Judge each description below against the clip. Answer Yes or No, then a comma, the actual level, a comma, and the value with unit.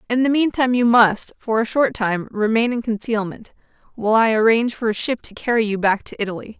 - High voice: Yes, high, 225 Hz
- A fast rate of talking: Yes, fast, 220 wpm